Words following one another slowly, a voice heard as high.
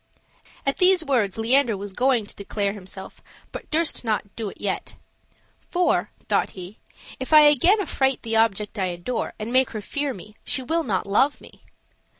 No: average, 175 wpm; high, 230 Hz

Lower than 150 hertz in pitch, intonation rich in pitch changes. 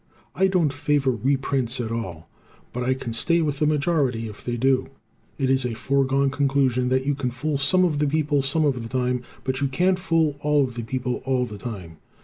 No: low, 135 Hz; average, 2.7 semitones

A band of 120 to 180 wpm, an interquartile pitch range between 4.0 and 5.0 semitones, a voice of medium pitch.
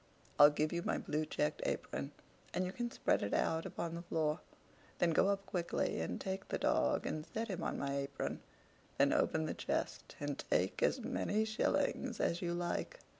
No: average, 190 wpm; average, 4.6 semitones; medium, 170 Hz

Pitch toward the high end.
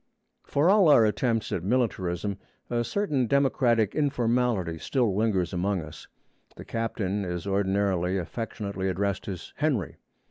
No: low, 105 Hz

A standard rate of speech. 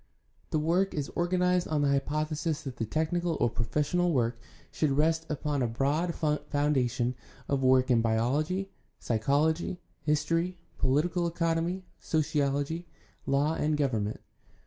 No: slow, 130 wpm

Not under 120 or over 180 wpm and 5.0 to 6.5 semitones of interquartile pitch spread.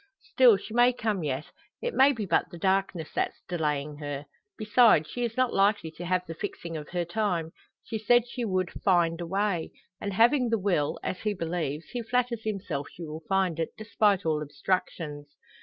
No: average, 190 wpm; average, 5.3 semitones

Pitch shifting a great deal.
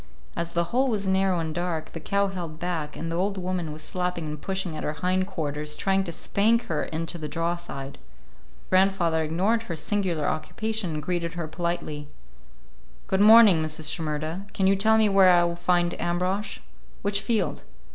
No: average, 3.4 semitones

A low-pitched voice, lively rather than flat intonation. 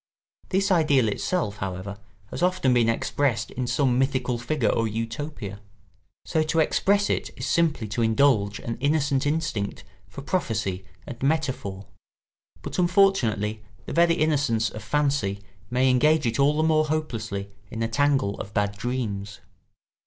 Yes: low, 130 Hz; wide, 6.1 semitones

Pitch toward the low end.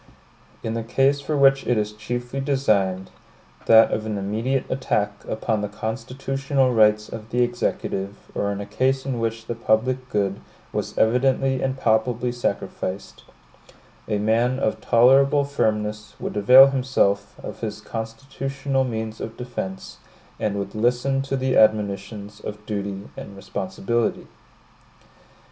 Yes: low, 115 Hz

